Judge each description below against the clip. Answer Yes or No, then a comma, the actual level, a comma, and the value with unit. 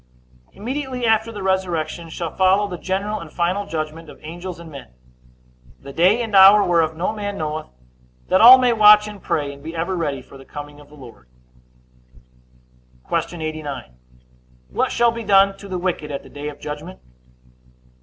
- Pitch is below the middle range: No, medium, 175 Hz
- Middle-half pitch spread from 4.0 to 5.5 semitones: Yes, average, 4.8 semitones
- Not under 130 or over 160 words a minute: No, average, 180 wpm